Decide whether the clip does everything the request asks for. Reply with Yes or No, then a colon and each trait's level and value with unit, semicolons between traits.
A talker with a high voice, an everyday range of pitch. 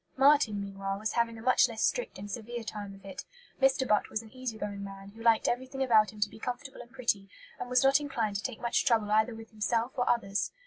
Yes: high, 225 Hz; average, 3.3 semitones